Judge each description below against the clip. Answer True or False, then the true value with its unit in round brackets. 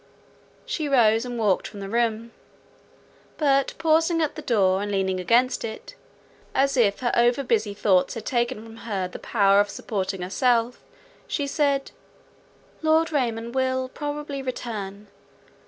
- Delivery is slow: False (145 wpm)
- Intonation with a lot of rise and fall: False (5.0 semitones)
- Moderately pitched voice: False (235 Hz)